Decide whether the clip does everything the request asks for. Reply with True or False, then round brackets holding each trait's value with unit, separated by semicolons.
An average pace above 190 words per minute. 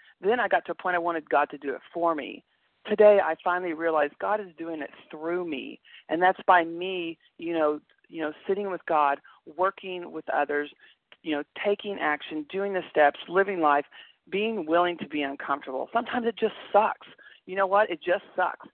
True (200 wpm)